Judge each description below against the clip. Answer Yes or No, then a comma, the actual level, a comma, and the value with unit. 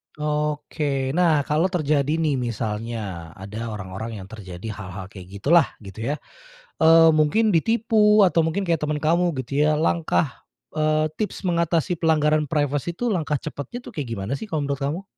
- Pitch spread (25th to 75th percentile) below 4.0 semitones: No, average, 4.9 semitones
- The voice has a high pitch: No, medium, 150 Hz